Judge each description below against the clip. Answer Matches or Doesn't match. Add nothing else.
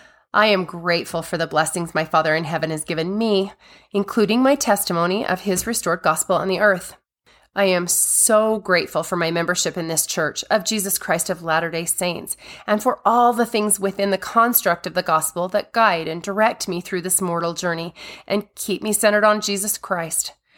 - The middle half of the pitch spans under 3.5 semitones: Doesn't match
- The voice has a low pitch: Doesn't match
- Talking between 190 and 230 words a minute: Matches